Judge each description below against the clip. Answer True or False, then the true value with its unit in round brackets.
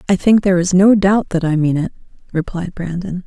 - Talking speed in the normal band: False (220 wpm)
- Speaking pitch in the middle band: True (180 Hz)